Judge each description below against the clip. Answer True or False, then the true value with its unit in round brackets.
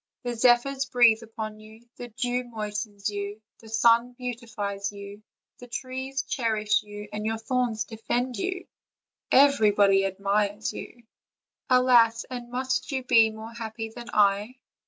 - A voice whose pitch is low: False (225 Hz)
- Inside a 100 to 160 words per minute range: True (140 wpm)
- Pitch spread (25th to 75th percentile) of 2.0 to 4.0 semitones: True (2.7 semitones)